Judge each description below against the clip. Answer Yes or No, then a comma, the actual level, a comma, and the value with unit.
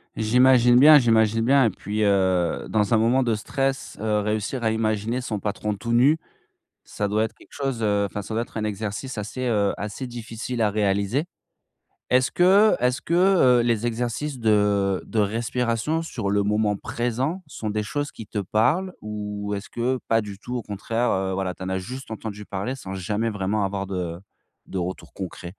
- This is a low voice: Yes, low, 110 Hz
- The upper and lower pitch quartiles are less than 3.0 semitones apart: No, average, 3.3 semitones